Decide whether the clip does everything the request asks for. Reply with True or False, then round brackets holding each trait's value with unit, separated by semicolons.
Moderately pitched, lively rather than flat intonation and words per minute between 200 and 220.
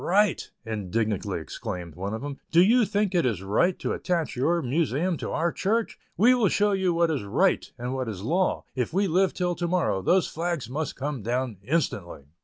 True (155 Hz; 8.3 semitones; 205 wpm)